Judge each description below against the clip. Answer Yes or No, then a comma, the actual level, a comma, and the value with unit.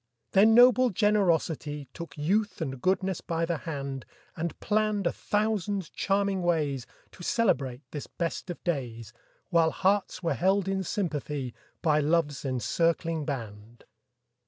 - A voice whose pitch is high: No, medium, 170 Hz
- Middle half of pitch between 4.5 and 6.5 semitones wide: Yes, average, 5.2 semitones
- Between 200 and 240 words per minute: No, slow, 135 wpm